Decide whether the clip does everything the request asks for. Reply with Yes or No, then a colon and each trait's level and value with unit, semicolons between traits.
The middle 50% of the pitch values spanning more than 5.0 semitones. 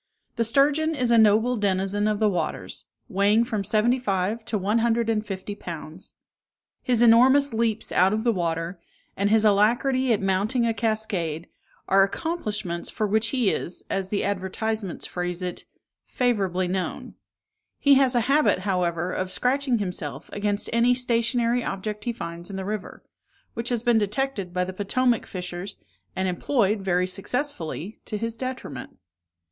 No: average, 4.0 semitones